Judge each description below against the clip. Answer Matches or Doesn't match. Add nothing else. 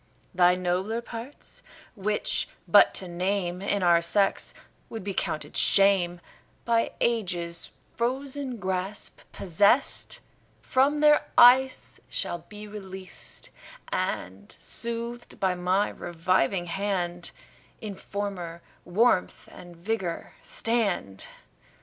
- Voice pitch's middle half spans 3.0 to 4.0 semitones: Doesn't match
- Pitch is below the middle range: Doesn't match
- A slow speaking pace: Matches